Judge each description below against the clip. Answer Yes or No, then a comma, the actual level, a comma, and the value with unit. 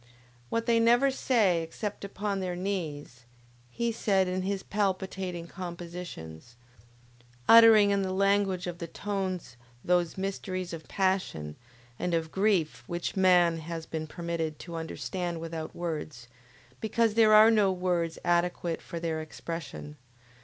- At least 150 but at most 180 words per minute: No, slow, 135 wpm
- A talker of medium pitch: Yes, medium, 180 Hz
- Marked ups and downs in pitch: No, average, 3.2 semitones